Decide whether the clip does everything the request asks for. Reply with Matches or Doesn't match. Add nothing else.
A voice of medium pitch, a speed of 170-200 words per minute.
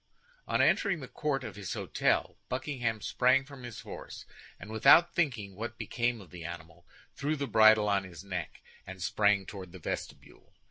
Doesn't match